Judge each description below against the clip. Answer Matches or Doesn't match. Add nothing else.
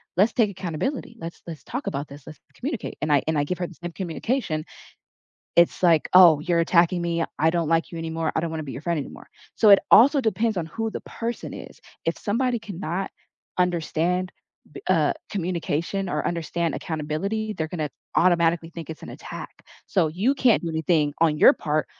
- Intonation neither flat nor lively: Matches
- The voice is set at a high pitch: Doesn't match